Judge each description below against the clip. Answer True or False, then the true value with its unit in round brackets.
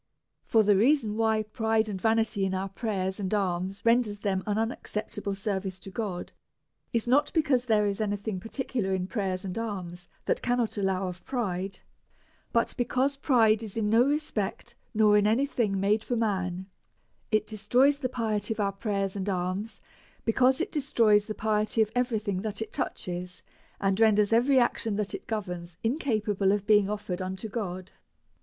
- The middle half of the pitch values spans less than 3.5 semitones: True (2.8 semitones)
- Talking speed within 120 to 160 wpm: False (175 wpm)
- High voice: True (210 Hz)